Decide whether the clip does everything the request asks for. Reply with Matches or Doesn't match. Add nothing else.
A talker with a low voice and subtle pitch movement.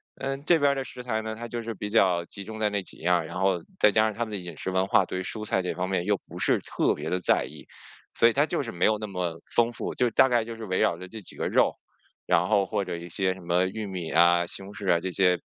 Doesn't match